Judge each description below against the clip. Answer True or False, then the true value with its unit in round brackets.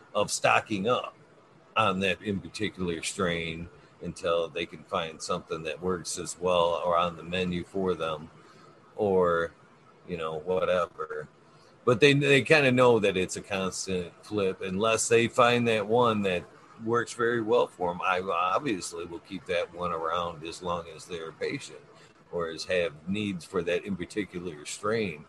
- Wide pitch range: True (6.0 semitones)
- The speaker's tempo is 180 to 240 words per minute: False (165 wpm)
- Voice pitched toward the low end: True (100 Hz)